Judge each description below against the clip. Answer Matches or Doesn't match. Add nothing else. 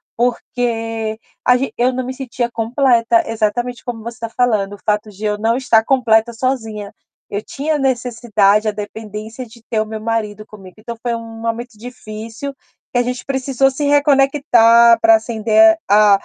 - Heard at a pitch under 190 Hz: Doesn't match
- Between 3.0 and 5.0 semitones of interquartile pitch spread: Doesn't match